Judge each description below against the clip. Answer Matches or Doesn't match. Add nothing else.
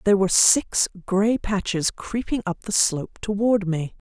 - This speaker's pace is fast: Doesn't match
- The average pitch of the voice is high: Matches